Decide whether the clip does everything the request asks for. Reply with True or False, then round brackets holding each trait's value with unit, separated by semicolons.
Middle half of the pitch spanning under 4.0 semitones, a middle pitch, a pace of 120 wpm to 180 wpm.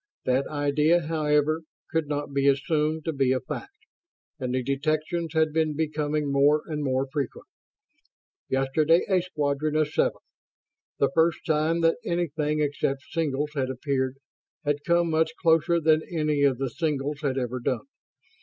True (2.5 semitones; 150 Hz; 155 wpm)